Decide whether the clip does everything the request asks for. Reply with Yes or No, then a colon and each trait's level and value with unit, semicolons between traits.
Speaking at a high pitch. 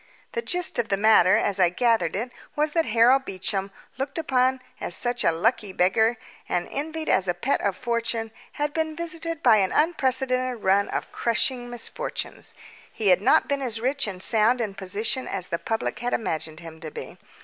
Yes: high, 230 Hz